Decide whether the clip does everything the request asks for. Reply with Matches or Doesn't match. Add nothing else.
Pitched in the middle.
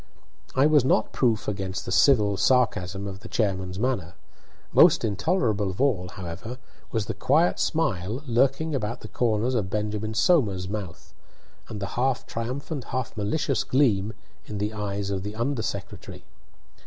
Doesn't match